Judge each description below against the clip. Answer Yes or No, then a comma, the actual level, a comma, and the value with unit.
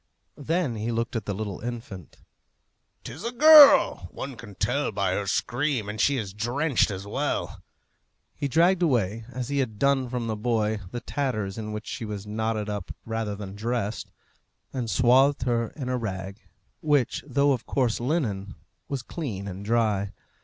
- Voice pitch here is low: Yes, low, 115 Hz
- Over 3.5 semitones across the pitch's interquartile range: Yes, average, 4.5 semitones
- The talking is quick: No, average, 175 wpm